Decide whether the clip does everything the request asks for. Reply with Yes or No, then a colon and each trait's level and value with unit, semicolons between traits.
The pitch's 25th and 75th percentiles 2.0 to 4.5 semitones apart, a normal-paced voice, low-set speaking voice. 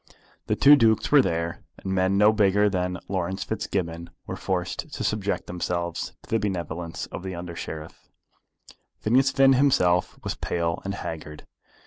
Yes: average, 3.8 semitones; average, 150 wpm; very low, 95 Hz